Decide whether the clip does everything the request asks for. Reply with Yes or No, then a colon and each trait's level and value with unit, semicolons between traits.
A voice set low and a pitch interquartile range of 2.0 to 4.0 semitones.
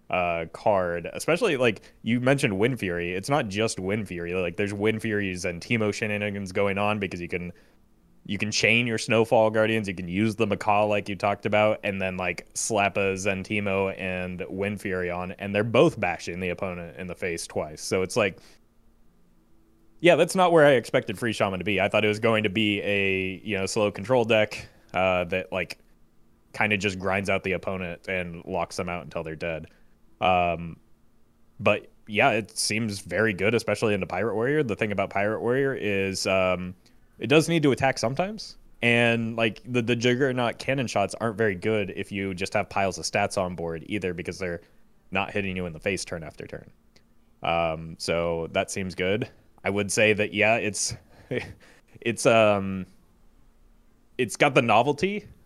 Yes: low, 100 Hz; average, 3.2 semitones